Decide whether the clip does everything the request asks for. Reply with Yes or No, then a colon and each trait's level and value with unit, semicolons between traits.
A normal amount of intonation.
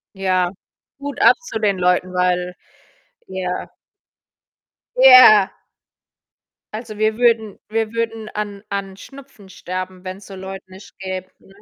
Yes: average, 3.0 semitones